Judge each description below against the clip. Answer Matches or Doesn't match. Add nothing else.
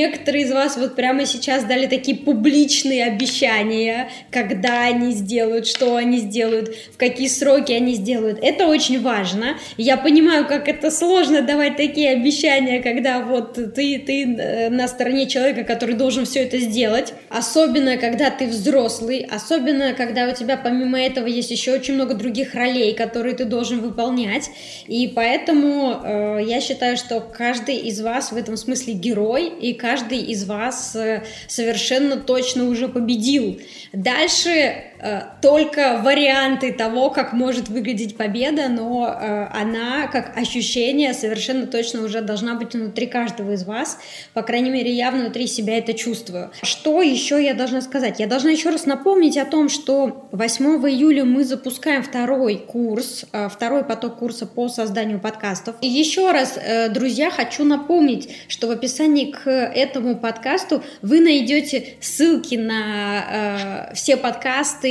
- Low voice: Doesn't match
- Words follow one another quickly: Doesn't match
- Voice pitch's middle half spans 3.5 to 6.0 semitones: Doesn't match